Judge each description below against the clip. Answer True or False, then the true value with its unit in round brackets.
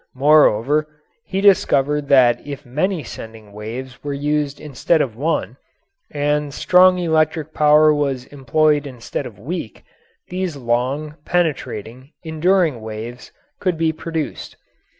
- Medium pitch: True (145 Hz)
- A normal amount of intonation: True (3.8 semitones)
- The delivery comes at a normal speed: False (120 wpm)